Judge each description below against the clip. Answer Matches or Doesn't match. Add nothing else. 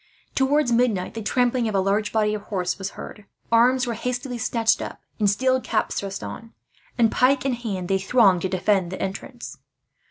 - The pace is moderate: Matches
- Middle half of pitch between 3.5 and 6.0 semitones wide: Matches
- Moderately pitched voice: Doesn't match